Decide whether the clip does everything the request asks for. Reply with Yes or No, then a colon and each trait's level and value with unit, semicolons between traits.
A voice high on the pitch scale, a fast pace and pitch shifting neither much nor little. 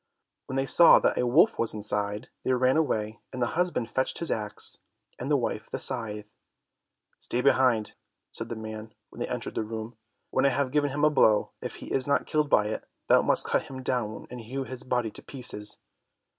No: low, 125 Hz; fast, 210 wpm; average, 3.7 semitones